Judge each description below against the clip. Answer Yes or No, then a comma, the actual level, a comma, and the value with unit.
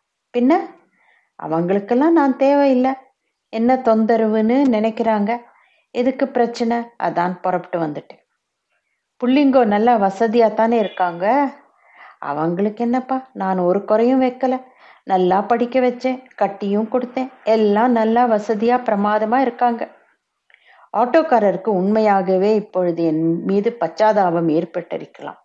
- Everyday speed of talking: Yes, average, 90 wpm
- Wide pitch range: No, average, 4.3 semitones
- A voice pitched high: Yes, high, 225 Hz